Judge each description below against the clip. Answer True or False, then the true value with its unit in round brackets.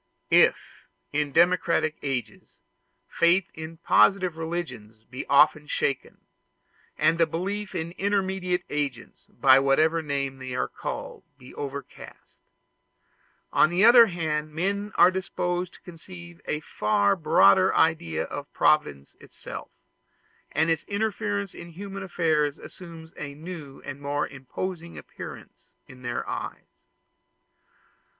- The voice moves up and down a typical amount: True (4.1 semitones)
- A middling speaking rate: False (120 wpm)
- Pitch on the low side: False (160 Hz)